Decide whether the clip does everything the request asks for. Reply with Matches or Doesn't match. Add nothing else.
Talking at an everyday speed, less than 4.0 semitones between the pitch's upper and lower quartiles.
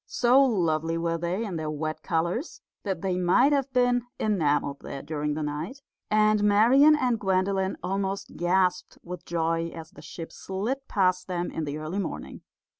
Doesn't match